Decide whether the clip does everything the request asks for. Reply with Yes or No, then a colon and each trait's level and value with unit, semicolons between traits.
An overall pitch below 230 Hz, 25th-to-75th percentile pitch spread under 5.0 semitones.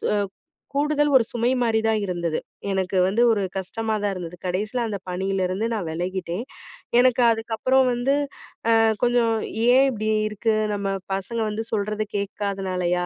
Yes: high, 210 Hz; average, 3.6 semitones